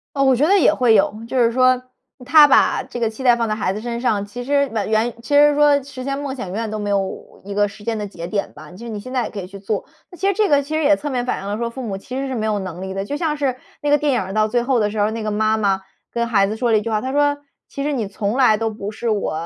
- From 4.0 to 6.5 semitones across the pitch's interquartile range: Yes, average, 4.7 semitones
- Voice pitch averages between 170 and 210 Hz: No, high, 230 Hz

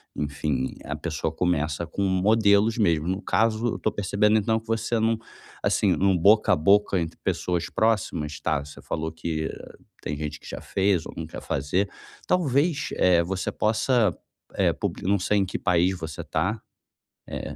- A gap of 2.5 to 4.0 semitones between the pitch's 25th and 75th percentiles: No, average, 5.0 semitones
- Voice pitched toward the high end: No, very low, 95 Hz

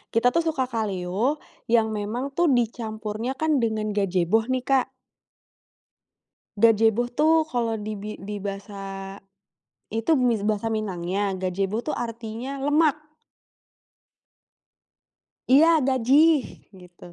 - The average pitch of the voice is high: Yes, high, 225 Hz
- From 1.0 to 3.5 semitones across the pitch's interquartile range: No, average, 4.2 semitones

